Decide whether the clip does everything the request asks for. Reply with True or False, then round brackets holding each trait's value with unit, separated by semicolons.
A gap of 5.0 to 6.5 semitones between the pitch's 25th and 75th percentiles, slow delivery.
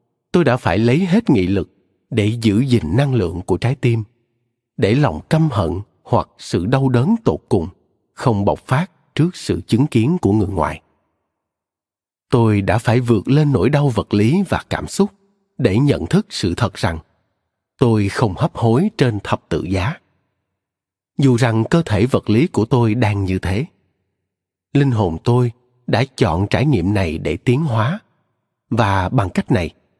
False (5.5 semitones; 175 wpm)